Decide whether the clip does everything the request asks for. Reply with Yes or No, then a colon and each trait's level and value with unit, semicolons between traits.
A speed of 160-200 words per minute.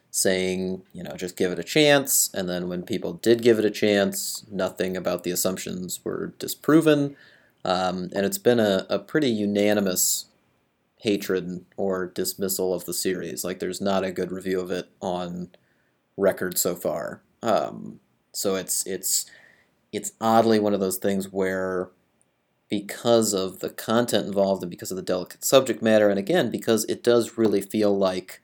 Yes: average, 170 wpm